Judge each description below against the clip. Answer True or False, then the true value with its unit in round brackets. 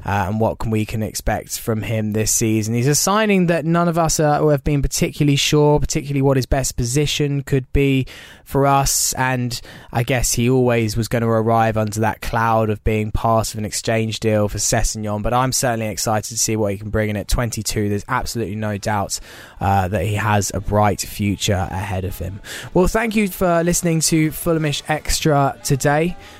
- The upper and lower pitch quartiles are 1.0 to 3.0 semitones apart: False (5.0 semitones)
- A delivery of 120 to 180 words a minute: False (200 wpm)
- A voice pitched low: True (115 Hz)